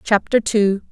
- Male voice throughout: No, female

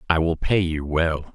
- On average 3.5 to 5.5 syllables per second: Yes, 4.3 syllables/s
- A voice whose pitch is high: No, very low, 80 Hz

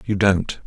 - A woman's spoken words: No, male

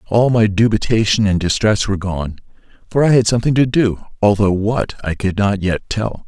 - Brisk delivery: No, average, 190 wpm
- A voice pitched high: No, low, 105 Hz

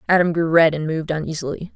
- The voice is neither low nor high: Yes, medium, 160 Hz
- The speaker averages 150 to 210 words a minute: Yes, fast, 205 wpm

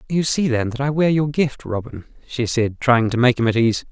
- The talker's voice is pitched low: Yes, low, 125 Hz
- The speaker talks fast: Yes, fast, 260 wpm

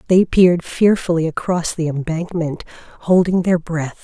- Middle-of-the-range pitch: Yes, medium, 170 Hz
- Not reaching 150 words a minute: Yes, slow, 135 wpm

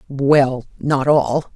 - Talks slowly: Yes, slow, 115 wpm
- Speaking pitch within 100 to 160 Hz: Yes, medium, 140 Hz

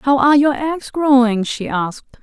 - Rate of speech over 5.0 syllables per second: No, 4.8 syllables/s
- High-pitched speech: Yes, very high, 260 Hz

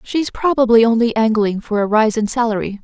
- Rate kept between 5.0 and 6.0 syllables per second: Yes, 5.5 syllables/s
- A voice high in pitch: Yes, high, 225 Hz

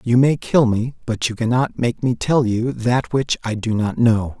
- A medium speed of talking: No, fast, 230 wpm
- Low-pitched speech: Yes, low, 120 Hz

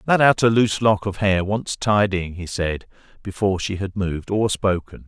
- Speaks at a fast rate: No, average, 190 wpm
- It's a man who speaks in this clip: Yes, male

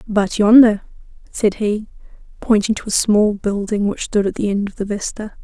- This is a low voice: No, high, 210 Hz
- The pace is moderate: Yes, average, 190 wpm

